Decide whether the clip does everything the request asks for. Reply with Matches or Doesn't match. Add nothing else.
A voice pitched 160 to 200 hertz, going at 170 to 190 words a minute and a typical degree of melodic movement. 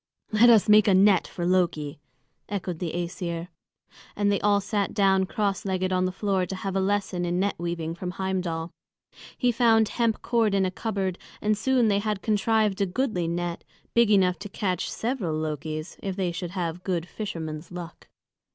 Matches